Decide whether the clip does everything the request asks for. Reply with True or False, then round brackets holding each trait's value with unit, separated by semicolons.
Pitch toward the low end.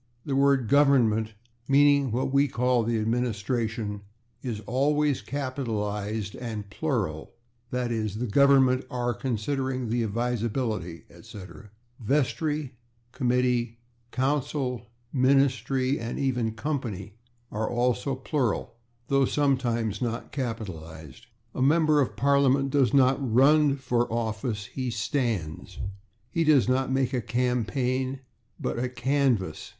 True (125 Hz)